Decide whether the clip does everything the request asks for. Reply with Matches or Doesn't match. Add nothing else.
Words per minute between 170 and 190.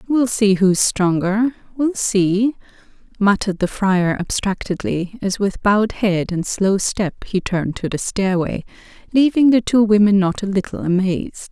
Doesn't match